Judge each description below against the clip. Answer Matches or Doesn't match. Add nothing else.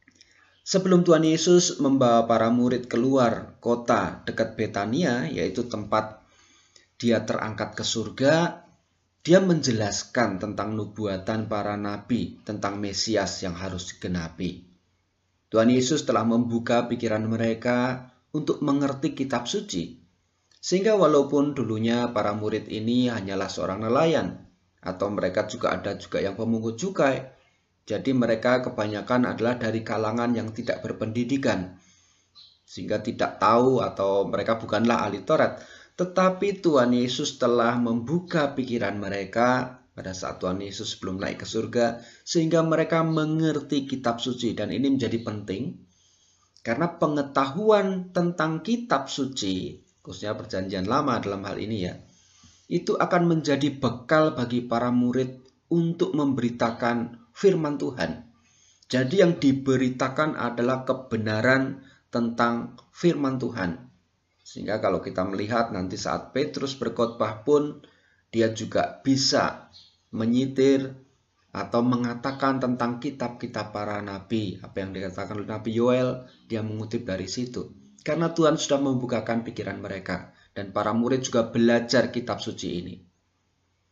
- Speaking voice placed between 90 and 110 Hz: Doesn't match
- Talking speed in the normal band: Matches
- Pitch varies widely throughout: Doesn't match